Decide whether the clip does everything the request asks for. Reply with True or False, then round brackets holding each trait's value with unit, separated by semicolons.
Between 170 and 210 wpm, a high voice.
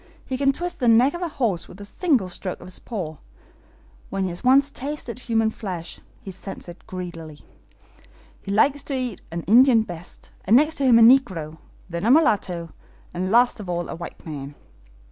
True (195 wpm; 210 Hz)